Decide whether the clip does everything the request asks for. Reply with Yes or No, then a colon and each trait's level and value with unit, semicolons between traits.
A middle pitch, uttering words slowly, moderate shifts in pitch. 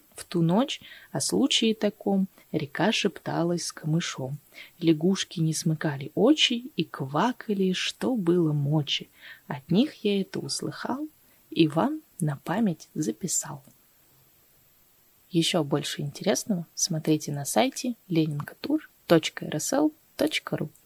No: medium, 175 Hz; slow, 105 wpm; wide, 6.2 semitones